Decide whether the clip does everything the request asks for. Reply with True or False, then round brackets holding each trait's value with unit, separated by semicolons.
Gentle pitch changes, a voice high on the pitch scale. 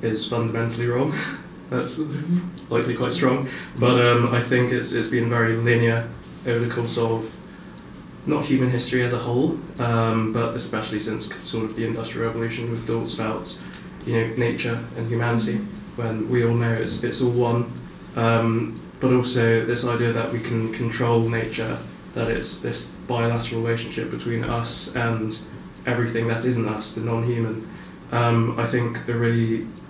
False (1.0 semitones; 115 Hz)